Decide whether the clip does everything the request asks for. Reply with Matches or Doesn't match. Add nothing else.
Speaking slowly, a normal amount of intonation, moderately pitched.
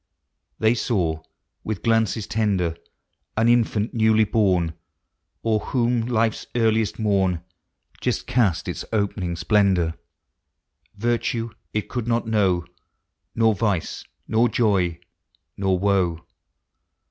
Doesn't match